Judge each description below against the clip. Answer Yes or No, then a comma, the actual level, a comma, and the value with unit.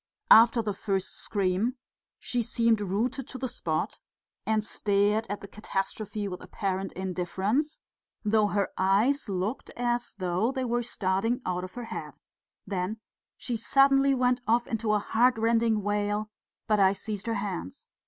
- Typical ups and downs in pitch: Yes, average, 3.5 semitones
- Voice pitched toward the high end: Yes, high, 215 Hz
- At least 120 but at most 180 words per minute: Yes, average, 155 wpm